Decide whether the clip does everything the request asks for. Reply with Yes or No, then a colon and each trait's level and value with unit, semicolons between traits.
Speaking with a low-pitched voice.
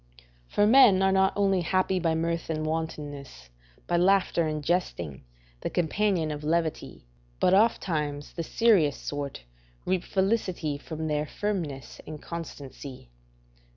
No: medium, 165 Hz